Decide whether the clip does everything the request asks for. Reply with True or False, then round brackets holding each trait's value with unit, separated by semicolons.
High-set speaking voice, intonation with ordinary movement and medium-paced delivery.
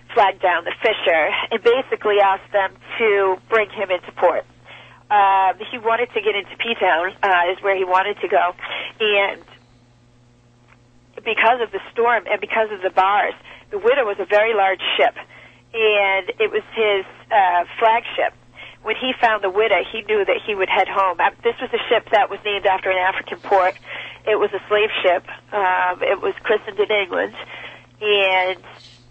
True (205 Hz; 3.2 semitones; 175 wpm)